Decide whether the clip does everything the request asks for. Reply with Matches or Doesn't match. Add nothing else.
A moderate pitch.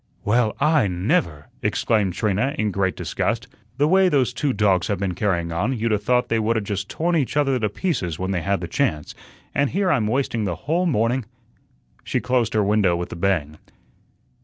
Doesn't match